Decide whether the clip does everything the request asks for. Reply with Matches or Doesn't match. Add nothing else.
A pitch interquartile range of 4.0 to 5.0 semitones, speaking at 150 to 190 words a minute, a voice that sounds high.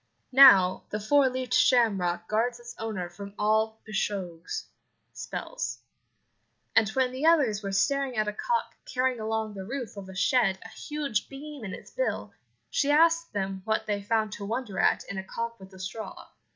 Matches